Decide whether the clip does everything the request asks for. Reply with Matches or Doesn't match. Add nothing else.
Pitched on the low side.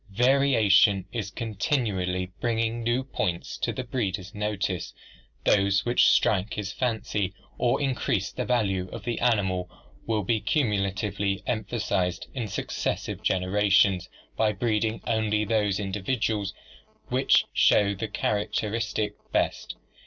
Matches